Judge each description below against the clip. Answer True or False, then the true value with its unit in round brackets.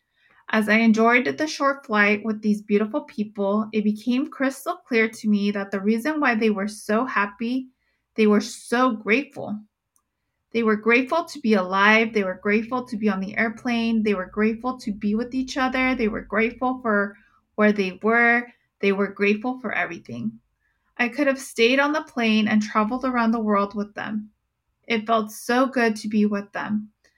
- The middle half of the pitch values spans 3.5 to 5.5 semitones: False (2.8 semitones)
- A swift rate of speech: False (185 wpm)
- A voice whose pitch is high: True (220 Hz)